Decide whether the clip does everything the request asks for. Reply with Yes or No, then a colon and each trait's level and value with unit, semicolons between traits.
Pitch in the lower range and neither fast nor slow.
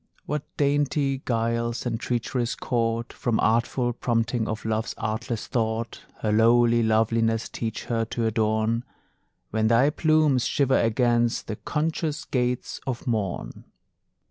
No: low, 115 Hz; slow, 125 wpm